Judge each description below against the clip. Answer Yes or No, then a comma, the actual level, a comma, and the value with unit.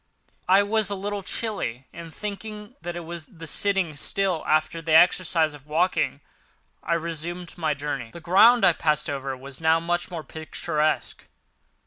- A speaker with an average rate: Yes, average, 160 wpm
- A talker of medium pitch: Yes, medium, 170 Hz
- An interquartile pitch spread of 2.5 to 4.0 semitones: Yes, average, 3.4 semitones